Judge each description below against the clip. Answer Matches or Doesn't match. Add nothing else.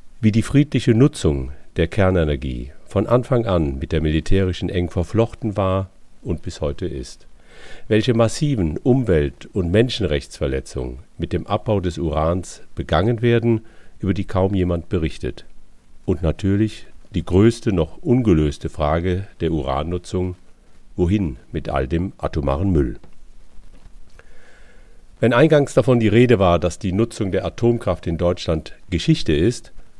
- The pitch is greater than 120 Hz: Doesn't match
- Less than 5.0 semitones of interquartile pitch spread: Doesn't match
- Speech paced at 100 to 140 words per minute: Matches